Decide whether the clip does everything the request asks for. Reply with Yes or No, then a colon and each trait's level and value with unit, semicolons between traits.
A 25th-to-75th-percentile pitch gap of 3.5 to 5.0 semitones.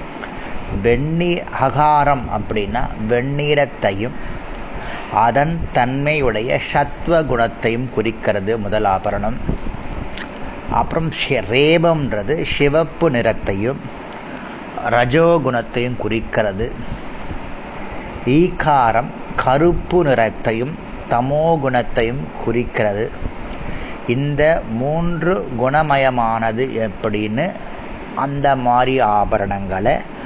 Yes: average, 4.7 semitones